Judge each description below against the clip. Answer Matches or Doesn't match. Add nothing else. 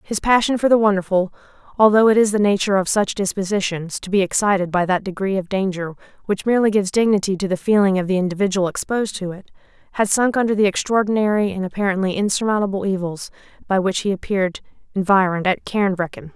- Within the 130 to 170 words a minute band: Doesn't match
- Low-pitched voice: Doesn't match